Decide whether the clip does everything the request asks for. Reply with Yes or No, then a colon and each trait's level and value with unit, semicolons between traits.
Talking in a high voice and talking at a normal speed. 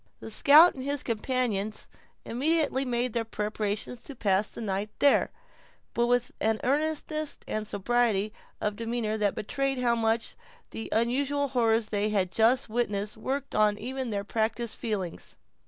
Yes: high, 230 Hz; average, 150 wpm